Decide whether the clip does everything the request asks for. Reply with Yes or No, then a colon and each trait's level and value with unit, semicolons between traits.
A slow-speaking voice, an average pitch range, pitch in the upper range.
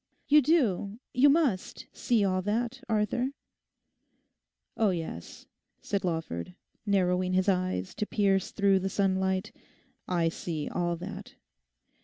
Yes: slow, 120 wpm; average, 3.0 semitones; high, 195 Hz